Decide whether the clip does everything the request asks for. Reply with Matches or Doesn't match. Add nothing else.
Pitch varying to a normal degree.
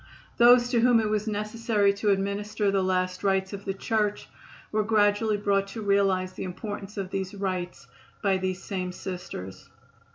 Doesn't match